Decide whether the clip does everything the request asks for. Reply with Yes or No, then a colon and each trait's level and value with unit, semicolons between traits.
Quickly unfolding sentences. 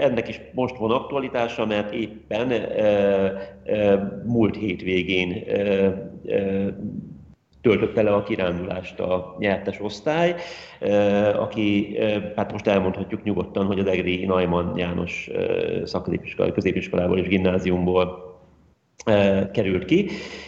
No: average, 110 wpm